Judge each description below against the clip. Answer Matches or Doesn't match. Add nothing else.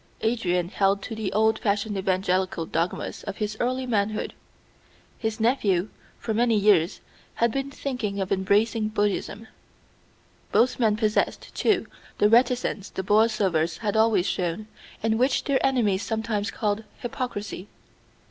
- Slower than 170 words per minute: Matches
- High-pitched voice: Matches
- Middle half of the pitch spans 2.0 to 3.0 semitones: Matches